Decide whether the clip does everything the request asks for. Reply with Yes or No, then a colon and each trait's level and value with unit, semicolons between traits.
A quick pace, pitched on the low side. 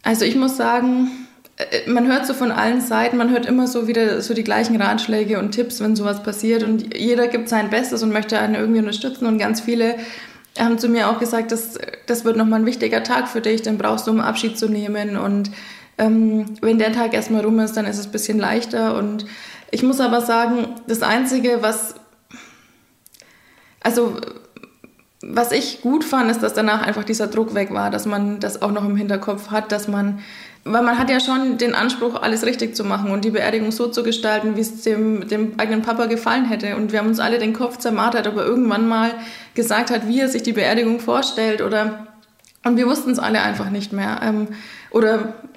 No: fast, 210 wpm; high, 225 Hz